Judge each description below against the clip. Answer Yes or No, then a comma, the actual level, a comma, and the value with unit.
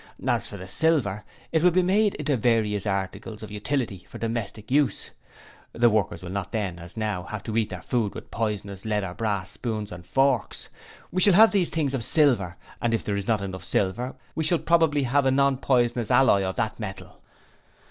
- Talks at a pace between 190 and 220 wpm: Yes, fast, 205 wpm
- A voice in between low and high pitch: No, low, 115 Hz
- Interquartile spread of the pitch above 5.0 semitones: Yes, wide, 5.6 semitones